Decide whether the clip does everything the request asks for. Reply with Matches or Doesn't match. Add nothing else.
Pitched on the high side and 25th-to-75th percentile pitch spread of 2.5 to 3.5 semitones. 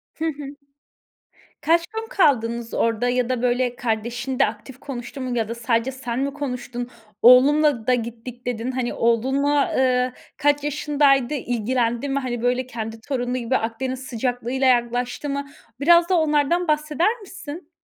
Matches